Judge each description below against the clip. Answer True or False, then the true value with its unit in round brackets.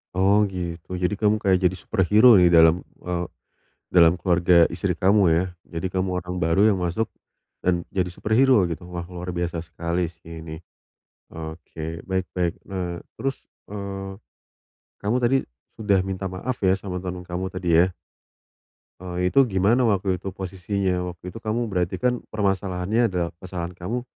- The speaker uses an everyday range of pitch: False (2.3 semitones)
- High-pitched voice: False (90 Hz)